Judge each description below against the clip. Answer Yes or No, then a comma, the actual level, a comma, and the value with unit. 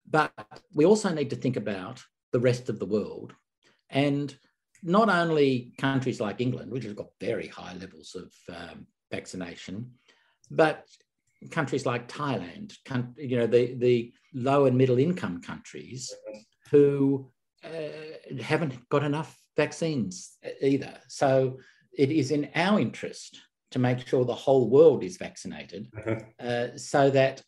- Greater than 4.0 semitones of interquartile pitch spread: No, average, 3.2 semitones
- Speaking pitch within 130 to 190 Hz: Yes, low, 135 Hz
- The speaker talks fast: No, average, 140 wpm